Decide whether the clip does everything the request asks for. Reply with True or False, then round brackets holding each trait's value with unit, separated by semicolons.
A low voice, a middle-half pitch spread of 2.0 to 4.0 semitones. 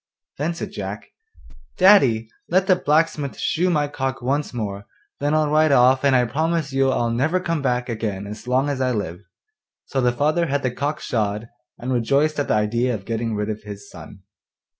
False (130 Hz; 4.7 semitones)